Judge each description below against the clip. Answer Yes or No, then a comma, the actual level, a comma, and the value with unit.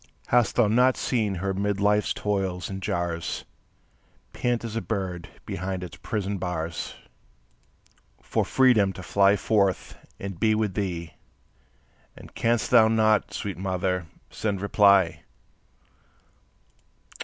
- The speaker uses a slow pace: Yes, slow, 120 wpm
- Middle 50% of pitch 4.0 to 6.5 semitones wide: No, average, 2.9 semitones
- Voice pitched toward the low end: Yes, low, 100 Hz